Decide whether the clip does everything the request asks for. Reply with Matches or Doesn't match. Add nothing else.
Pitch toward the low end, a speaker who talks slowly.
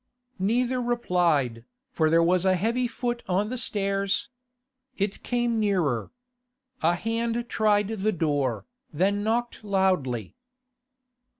Doesn't match